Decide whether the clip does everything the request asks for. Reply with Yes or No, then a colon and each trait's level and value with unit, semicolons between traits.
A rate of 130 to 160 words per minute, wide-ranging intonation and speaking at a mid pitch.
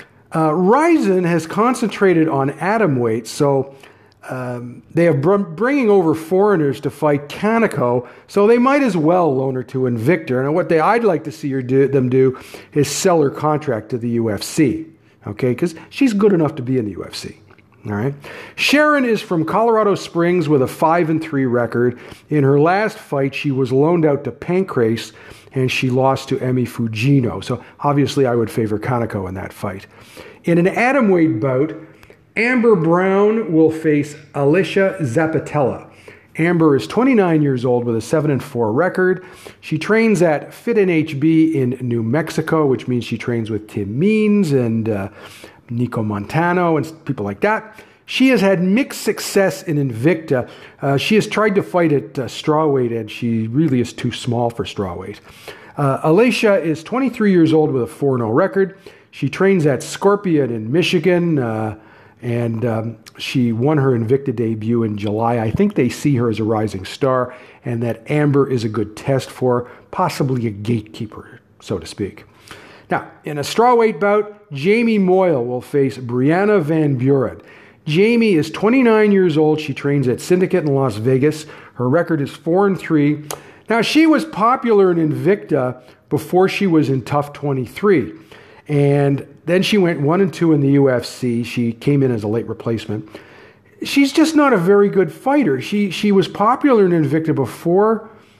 No: average, 175 wpm; wide, 6.9 semitones; medium, 145 Hz